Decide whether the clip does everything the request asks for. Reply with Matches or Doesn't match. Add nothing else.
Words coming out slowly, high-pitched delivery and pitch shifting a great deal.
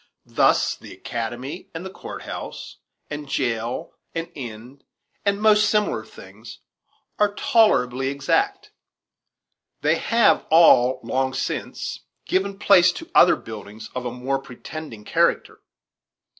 Doesn't match